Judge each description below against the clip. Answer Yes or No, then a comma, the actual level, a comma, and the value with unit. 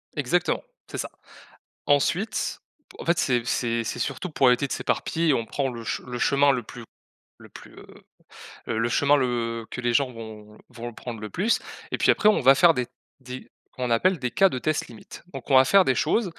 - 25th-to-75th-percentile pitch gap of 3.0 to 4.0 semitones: Yes, average, 3.6 semitones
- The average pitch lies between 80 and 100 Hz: No, low, 125 Hz